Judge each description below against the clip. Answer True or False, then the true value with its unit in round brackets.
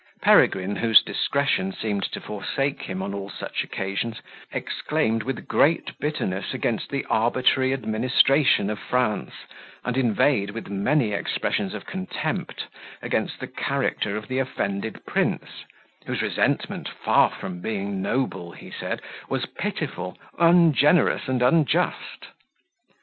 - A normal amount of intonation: True (5.0 semitones)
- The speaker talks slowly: True (125 wpm)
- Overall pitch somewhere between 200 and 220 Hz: False (110 Hz)